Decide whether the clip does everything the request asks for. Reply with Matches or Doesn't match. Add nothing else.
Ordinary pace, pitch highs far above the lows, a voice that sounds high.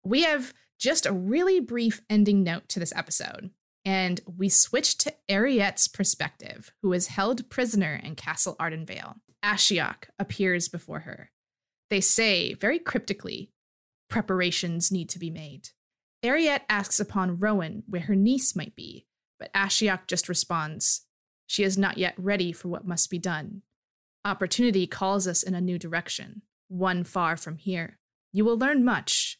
Doesn't match